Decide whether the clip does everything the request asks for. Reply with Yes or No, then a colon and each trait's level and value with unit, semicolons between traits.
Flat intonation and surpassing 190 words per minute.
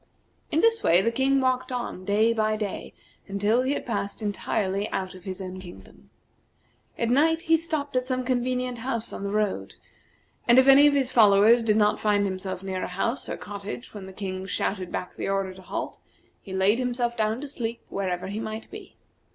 No: average, 4.5 semitones; average, 200 wpm